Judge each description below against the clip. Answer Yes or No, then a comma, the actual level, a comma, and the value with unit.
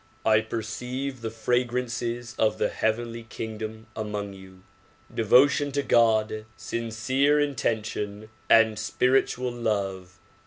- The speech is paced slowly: Yes, slow, 110 wpm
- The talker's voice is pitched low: Yes, low, 115 Hz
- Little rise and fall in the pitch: Yes, narrow, 2.3 semitones